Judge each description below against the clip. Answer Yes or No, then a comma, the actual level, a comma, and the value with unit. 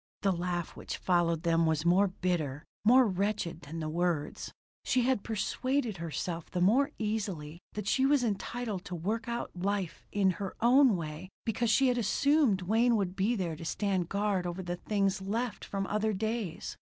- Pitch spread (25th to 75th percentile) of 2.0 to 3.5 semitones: No, average, 4.4 semitones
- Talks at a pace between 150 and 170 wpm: No, average, 180 wpm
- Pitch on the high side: Yes, high, 195 Hz